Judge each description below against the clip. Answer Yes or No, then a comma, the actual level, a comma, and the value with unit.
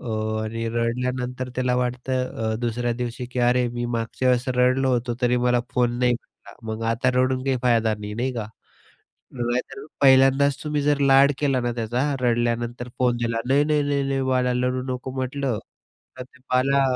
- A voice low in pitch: Yes, low, 125 Hz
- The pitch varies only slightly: Yes, narrow, 1.6 semitones